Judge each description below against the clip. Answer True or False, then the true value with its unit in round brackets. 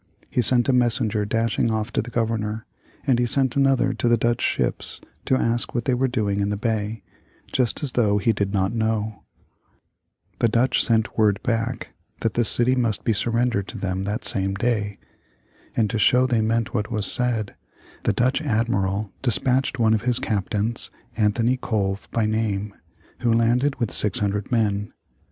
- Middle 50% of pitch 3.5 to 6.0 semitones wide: False (2.6 semitones)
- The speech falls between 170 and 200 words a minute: True (175 wpm)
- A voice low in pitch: True (115 Hz)